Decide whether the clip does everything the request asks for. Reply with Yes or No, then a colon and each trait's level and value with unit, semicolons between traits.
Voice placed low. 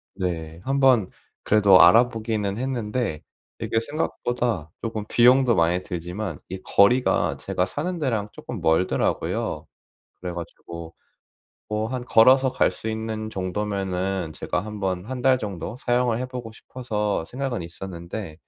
Yes: low, 105 Hz